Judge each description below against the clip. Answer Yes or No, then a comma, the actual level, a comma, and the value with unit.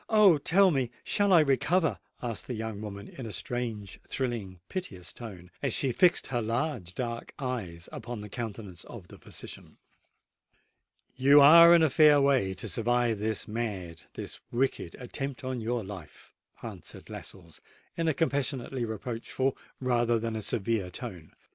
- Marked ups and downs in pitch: No, average, 4.7 semitones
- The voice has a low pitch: Yes, low, 120 Hz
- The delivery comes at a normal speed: Yes, average, 150 wpm